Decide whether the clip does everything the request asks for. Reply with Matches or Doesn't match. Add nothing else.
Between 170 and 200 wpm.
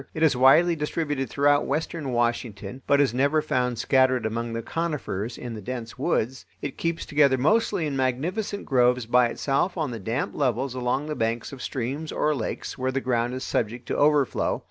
Matches